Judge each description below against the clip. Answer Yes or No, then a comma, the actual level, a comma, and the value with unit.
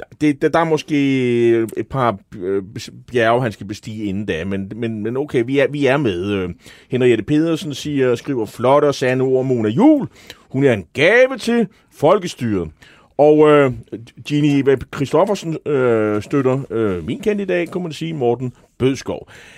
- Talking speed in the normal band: Yes, average, 160 wpm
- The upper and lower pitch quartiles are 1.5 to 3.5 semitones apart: No, average, 4.9 semitones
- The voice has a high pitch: No, low, 130 Hz